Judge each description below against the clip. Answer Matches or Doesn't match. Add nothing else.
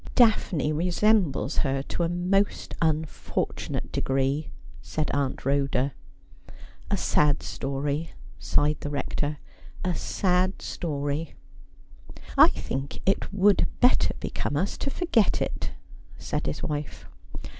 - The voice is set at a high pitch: Doesn't match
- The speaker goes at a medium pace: Doesn't match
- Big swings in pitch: Doesn't match